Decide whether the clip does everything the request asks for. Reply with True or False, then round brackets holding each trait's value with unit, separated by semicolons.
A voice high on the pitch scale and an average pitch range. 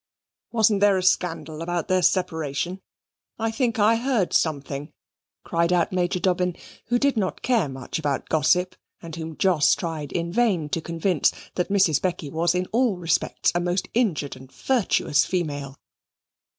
False (175 Hz; 3.7 semitones)